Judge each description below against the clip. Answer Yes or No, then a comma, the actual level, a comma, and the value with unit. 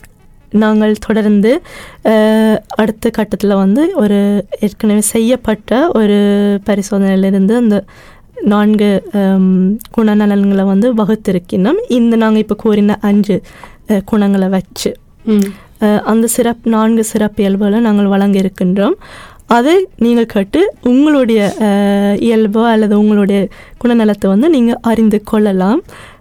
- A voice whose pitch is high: Yes, high, 210 Hz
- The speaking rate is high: No, average, 95 wpm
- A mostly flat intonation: Yes, narrow, 2.1 semitones